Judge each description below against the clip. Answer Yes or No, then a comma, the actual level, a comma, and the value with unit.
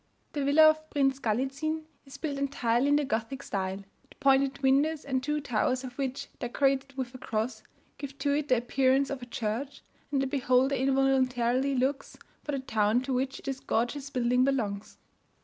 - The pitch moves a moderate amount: No, narrow, 2.1 semitones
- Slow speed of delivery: No, average, 180 wpm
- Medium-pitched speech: No, very high, 265 Hz